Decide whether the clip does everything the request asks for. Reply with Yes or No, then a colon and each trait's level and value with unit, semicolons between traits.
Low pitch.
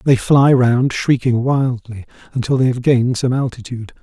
Yes: low, 125 Hz